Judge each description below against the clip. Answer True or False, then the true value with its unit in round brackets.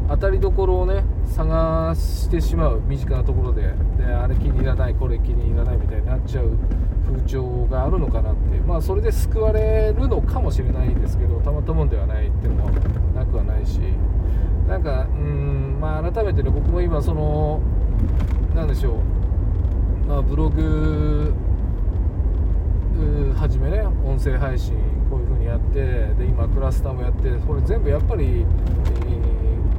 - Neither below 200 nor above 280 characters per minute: False (325 characters per minute)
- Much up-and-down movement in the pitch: False (2.9 semitones)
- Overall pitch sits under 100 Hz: True (80 Hz)